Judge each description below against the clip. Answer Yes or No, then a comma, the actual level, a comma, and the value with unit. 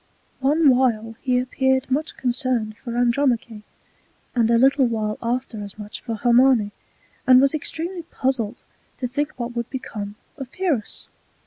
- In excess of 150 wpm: No, average, 145 wpm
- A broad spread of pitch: No, average, 2.8 semitones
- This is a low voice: No, very high, 250 Hz